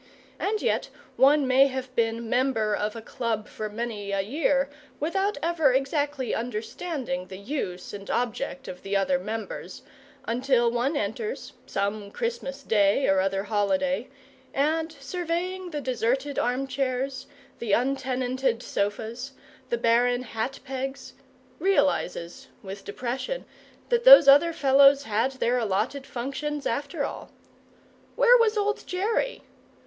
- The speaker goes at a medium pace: No, slow, 130 wpm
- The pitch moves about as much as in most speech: Yes, average, 4.5 semitones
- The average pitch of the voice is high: Yes, very high, 260 Hz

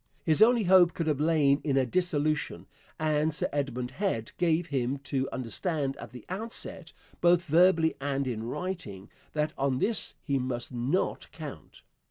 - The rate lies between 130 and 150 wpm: No, average, 160 wpm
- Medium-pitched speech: Yes, medium, 150 Hz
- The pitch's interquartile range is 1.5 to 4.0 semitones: No, average, 4.7 semitones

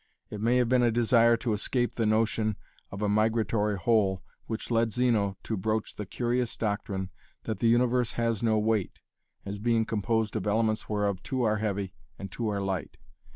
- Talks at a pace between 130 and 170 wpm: No, average, 185 wpm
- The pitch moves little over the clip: Yes, narrow, 2.2 semitones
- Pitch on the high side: No, low, 110 Hz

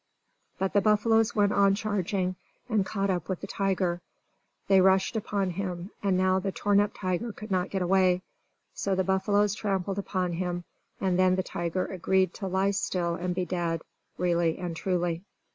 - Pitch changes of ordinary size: No, narrow, 1.9 semitones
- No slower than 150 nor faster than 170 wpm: No, average, 180 wpm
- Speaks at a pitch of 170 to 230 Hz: Yes, high, 190 Hz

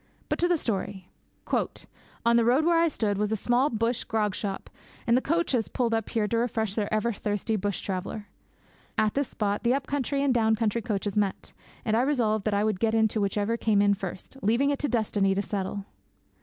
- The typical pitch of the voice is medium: No, high, 220 Hz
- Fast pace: Yes, fast, 210 wpm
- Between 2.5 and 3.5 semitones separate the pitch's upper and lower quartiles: Yes, average, 2.9 semitones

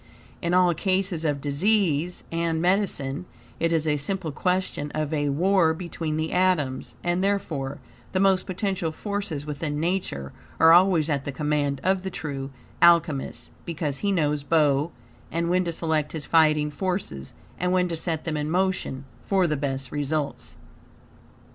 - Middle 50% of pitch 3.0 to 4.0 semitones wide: Yes, average, 3.7 semitones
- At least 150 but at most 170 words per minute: Yes, average, 160 wpm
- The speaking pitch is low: No, medium, 160 Hz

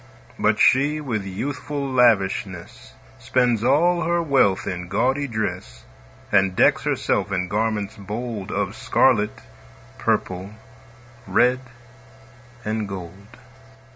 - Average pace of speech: No, slow, 105 wpm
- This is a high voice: No, low, 110 Hz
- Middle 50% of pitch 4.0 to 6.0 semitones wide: Yes, average, 5.2 semitones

